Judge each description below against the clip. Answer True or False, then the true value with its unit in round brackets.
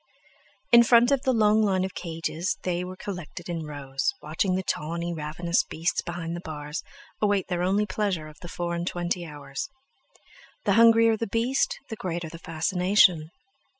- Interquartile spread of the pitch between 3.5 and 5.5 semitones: True (4.0 semitones)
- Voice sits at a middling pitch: True (175 Hz)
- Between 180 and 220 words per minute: False (170 wpm)